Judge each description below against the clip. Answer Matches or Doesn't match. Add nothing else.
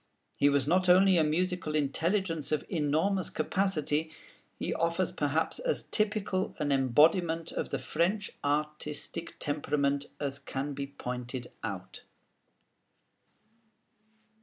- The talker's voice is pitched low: Doesn't match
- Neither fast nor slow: Doesn't match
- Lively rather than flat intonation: Doesn't match